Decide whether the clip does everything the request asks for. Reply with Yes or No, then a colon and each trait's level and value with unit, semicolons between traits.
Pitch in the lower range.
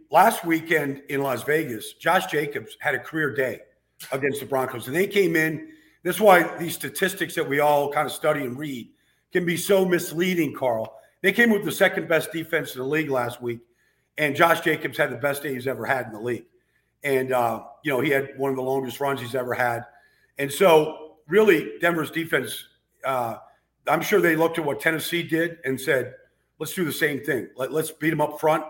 No: medium, 150 Hz